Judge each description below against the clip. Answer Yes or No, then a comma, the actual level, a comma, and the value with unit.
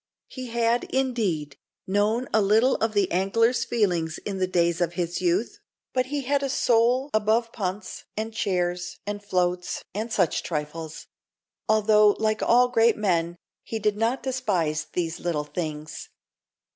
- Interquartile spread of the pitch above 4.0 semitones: Yes, average, 4.8 semitones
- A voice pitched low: No, high, 205 Hz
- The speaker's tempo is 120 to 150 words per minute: Yes, average, 145 wpm